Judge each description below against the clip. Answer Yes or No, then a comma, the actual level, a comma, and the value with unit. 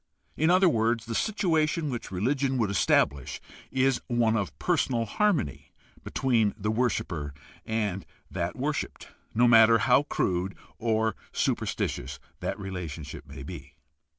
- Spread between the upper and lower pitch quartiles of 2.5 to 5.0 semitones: No, wide, 5.4 semitones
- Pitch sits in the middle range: No, low, 115 Hz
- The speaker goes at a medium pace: No, slow, 125 wpm